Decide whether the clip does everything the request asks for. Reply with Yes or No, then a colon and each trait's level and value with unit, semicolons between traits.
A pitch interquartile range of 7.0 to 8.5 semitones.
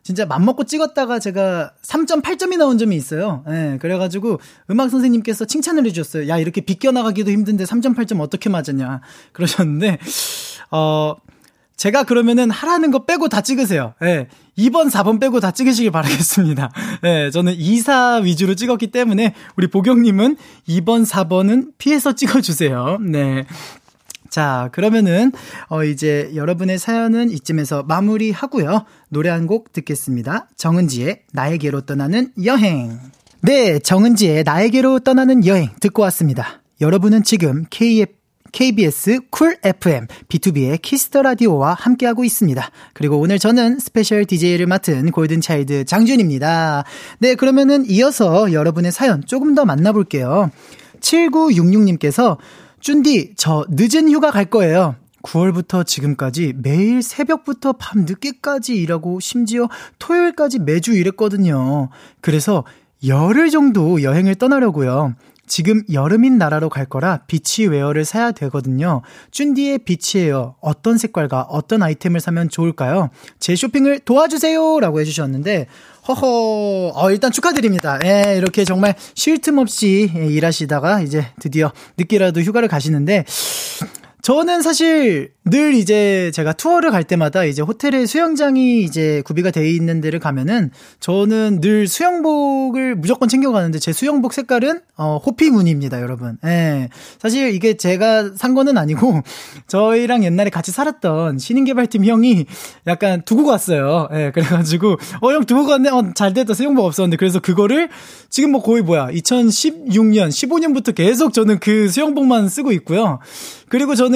Yes: wide, 7.5 semitones